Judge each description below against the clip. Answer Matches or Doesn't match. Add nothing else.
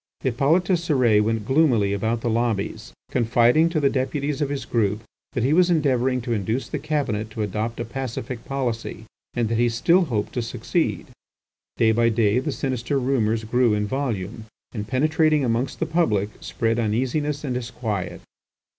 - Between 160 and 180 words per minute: Matches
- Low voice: Matches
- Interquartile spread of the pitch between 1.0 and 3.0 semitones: Doesn't match